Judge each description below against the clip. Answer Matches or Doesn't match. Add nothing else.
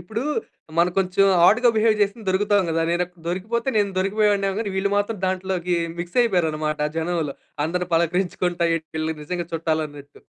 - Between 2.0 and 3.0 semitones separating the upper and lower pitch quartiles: Doesn't match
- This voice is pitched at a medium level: Matches